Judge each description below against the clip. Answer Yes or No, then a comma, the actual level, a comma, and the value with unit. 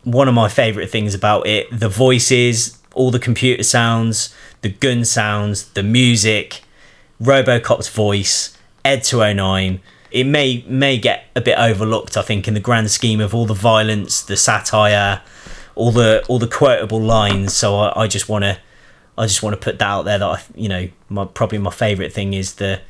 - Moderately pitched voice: No, low, 110 Hz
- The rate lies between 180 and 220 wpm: Yes, average, 185 wpm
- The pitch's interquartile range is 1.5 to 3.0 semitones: Yes, average, 2.7 semitones